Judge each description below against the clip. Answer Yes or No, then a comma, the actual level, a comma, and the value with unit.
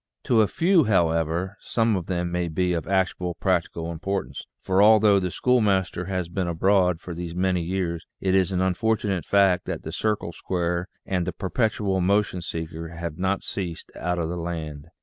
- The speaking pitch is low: Yes, very low, 90 Hz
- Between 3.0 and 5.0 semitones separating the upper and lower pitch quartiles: No, narrow, 2.4 semitones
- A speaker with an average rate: Yes, average, 185 wpm